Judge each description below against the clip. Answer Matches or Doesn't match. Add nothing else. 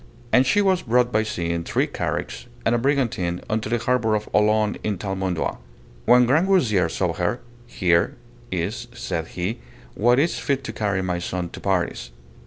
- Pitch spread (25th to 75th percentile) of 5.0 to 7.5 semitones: Matches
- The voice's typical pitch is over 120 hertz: Doesn't match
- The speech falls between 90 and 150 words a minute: Doesn't match